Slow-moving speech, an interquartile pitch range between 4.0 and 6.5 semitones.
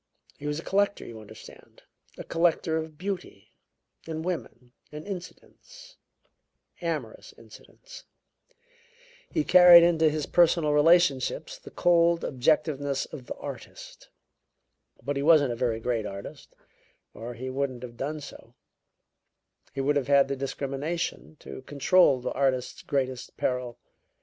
Yes: slow, 130 wpm; average, 4.6 semitones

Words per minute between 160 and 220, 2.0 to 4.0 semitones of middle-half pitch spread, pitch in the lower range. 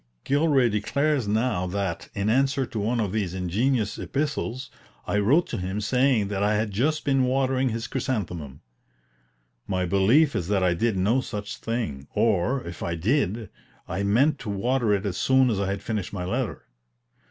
No: average, 175 wpm; average, 5.0 semitones; low, 110 Hz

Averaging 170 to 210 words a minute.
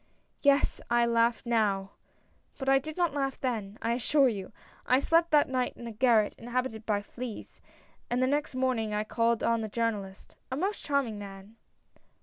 Yes: average, 190 wpm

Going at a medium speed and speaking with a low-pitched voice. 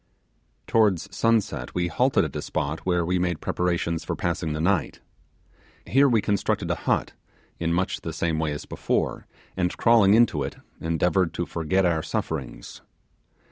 Yes: average, 160 wpm; very low, 85 Hz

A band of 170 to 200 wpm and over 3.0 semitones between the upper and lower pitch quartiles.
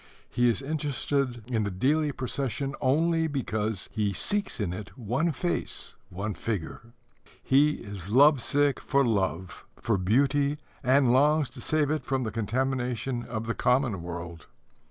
No: average, 150 wpm; average, 4.9 semitones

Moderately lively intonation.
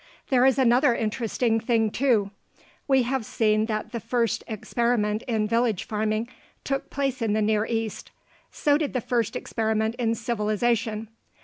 No: narrow, 2.2 semitones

